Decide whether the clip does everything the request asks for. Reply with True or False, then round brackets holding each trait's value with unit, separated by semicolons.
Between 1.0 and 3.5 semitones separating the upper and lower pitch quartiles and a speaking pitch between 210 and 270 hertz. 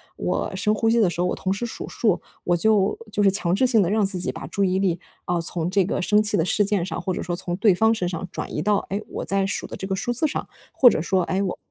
False (2.9 semitones; 195 Hz)